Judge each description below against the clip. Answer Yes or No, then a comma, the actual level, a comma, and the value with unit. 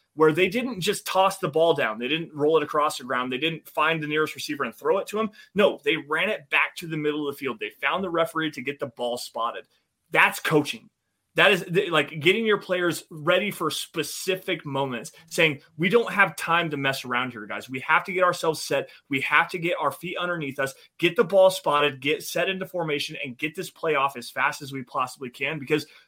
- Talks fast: Yes, fast, 235 wpm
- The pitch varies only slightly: No, average, 4.1 semitones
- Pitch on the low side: No, medium, 160 Hz